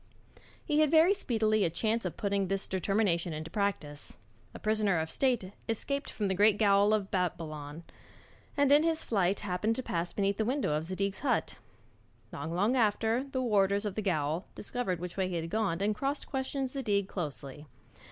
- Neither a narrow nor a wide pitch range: Yes, average, 4.4 semitones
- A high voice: Yes, high, 200 Hz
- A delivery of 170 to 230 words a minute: Yes, average, 180 wpm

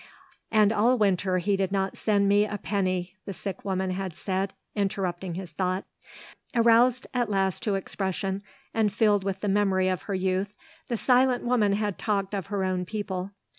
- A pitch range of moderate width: No, narrow, 1.9 semitones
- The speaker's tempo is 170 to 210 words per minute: Yes, average, 175 wpm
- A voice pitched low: No, high, 195 Hz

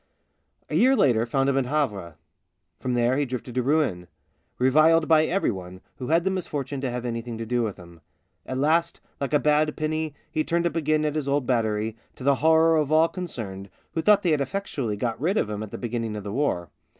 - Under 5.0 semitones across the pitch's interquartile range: No, average, 5.3 semitones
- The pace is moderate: No, fast, 230 wpm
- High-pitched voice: No, low, 135 Hz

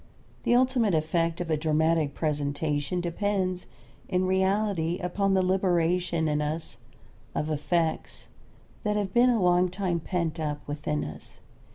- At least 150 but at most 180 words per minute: No, average, 140 wpm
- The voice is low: No, medium, 175 Hz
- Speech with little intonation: No, average, 3.2 semitones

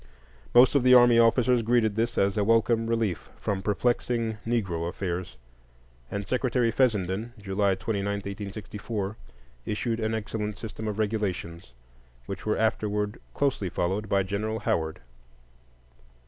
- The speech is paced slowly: Yes, slow, 130 wpm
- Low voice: Yes, low, 105 Hz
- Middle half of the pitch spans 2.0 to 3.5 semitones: Yes, narrow, 2.6 semitones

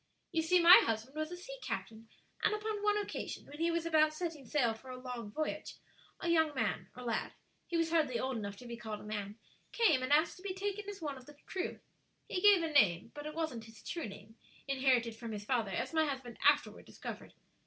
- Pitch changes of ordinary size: No, wide, 6.5 semitones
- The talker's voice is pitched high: Yes, very high, 290 Hz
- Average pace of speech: No, fast, 230 wpm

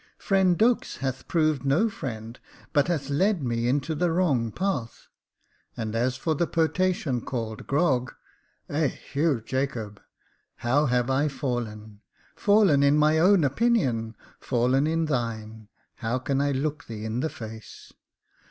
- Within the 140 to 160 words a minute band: Yes, average, 155 wpm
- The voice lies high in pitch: No, low, 135 Hz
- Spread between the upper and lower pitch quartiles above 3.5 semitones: Yes, average, 5.1 semitones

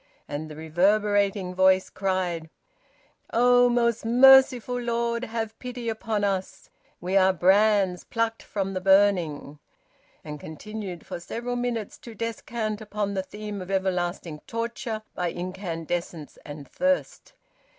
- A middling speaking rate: No, slow, 125 wpm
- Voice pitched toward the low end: No, high, 200 Hz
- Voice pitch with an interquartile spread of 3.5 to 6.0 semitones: Yes, average, 4.2 semitones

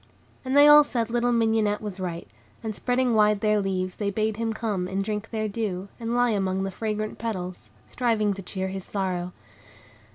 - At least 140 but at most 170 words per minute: No, average, 190 wpm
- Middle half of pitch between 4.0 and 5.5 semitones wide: No, average, 2.9 semitones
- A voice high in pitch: Yes, high, 210 Hz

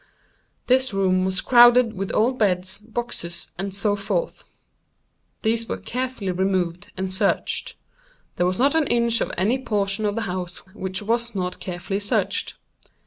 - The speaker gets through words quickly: No, average, 150 wpm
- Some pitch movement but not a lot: Yes, average, 3.9 semitones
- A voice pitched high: Yes, high, 200 Hz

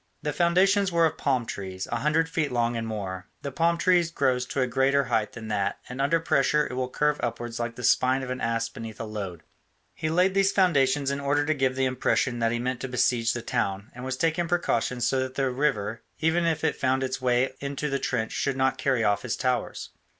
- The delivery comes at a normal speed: No, fast, 230 wpm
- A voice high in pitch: No, low, 130 Hz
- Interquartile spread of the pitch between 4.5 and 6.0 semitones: No, average, 4.0 semitones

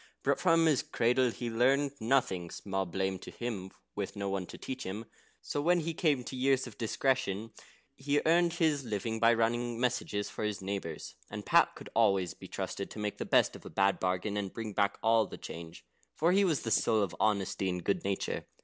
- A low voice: Yes, low, 115 Hz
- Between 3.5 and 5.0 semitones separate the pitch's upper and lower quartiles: No, wide, 5.4 semitones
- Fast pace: Yes, fast, 210 wpm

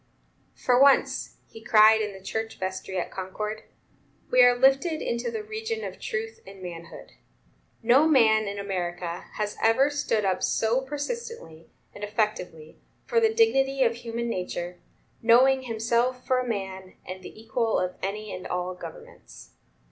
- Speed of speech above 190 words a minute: No, average, 155 wpm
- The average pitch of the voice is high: Yes, high, 225 Hz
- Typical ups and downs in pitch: No, wide, 5.8 semitones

